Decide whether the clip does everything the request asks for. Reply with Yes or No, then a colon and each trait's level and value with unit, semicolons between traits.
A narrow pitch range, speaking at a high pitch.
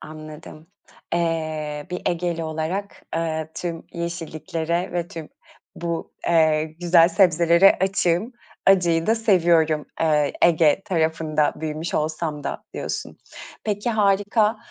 No: narrow, 2.2 semitones; medium, 165 Hz